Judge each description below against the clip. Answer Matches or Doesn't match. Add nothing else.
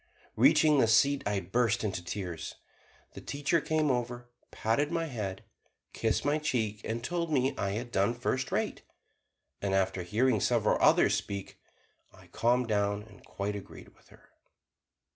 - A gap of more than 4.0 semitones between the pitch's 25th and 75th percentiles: Matches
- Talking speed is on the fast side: Doesn't match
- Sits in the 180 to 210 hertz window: Doesn't match